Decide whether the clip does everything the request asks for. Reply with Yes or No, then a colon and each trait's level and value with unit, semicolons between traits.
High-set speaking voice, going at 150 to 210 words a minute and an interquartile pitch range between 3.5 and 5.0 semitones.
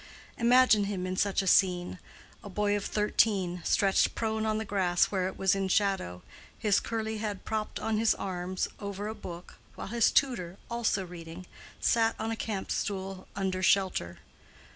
No: high, 200 Hz; average, 170 wpm; average, 2.8 semitones